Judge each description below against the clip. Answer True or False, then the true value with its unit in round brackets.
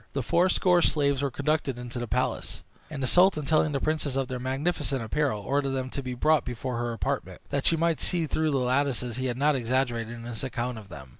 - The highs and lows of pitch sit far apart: False (3.7 semitones)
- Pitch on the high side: False (135 Hz)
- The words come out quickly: True (225 wpm)